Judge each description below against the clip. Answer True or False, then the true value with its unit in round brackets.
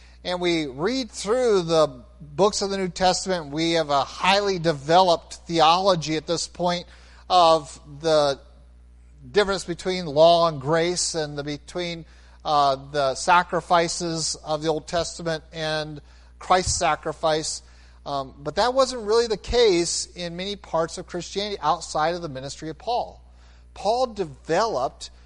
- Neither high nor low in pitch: True (165 Hz)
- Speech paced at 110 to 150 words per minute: True (140 wpm)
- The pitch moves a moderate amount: True (4.0 semitones)